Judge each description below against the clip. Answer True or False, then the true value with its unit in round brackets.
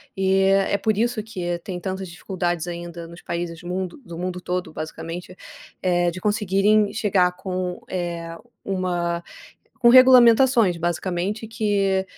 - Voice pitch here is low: False (185 Hz)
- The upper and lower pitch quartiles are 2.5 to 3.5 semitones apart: True (2.8 semitones)